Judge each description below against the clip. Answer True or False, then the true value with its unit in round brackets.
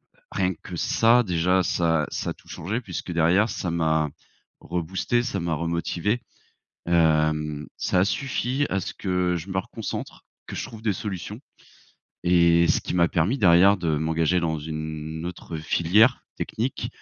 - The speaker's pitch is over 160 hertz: False (85 Hz)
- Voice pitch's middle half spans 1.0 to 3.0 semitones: False (3.4 semitones)